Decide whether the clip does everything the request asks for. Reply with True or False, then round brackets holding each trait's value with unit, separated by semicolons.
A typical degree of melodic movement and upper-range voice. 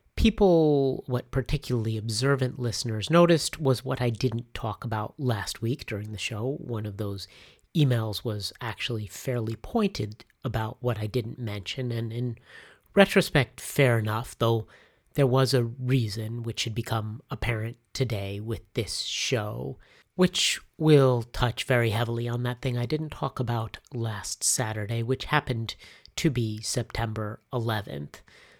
False (3.1 semitones; 120 Hz)